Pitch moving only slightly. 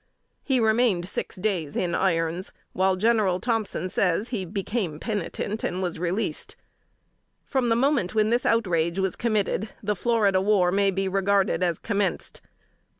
No: average, 3.5 semitones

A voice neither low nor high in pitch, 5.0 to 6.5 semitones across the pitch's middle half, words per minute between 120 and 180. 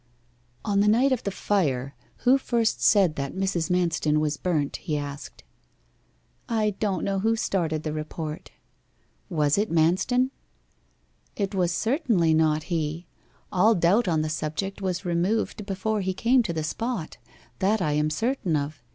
Yes: medium, 180 Hz; average, 5.3 semitones; average, 155 wpm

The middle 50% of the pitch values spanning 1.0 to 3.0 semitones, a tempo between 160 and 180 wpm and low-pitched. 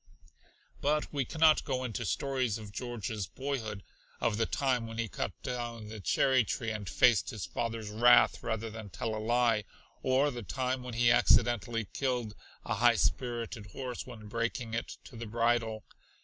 Yes: narrow, 2.4 semitones; average, 170 wpm; low, 115 Hz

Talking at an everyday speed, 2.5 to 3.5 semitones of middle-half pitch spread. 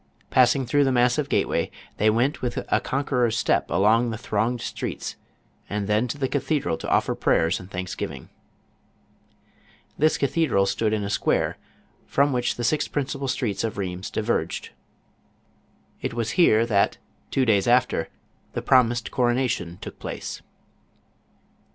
No: average, 145 wpm; average, 3.9 semitones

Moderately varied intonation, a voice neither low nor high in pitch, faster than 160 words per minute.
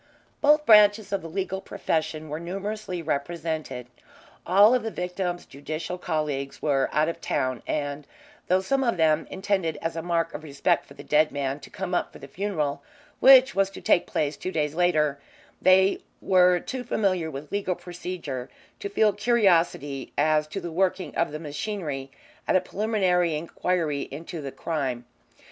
Yes: average, 4.2 semitones; medium, 170 Hz; average, 170 wpm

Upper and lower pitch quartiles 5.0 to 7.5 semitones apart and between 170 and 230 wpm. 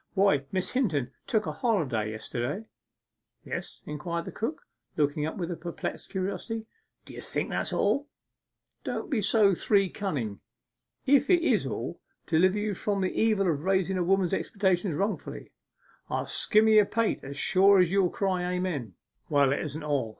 No: wide, 5.5 semitones; average, 160 wpm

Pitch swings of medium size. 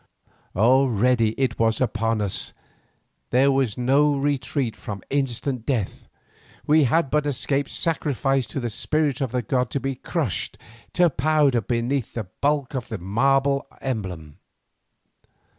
Yes: average, 3.5 semitones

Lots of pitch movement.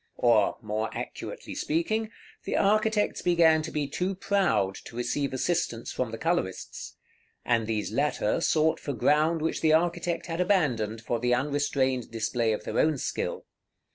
Yes: wide, 6.5 semitones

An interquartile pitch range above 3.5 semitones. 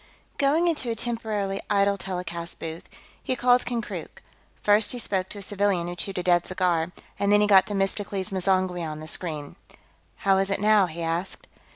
No: average, 2.8 semitones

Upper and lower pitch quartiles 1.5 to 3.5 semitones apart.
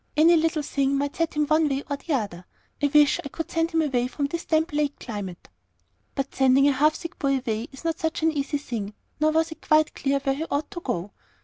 Yes: average, 2.8 semitones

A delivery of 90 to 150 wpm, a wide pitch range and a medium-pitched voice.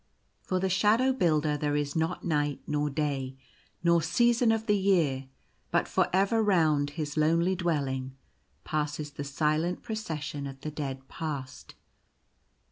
No: average, 140 wpm; average, 4.2 semitones; medium, 155 Hz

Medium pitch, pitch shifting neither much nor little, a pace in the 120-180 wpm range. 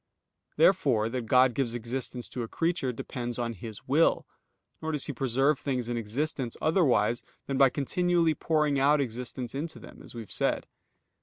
No: low, 130 Hz; average, 3.9 semitones; average, 170 wpm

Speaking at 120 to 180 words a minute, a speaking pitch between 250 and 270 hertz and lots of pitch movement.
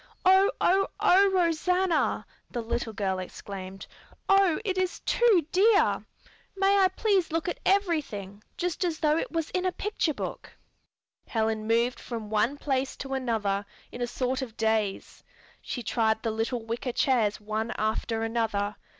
Yes: average, 155 wpm; very high, 255 Hz; wide, 8.6 semitones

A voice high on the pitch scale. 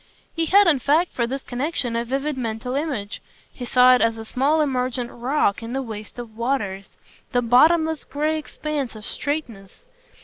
Yes: very high, 255 Hz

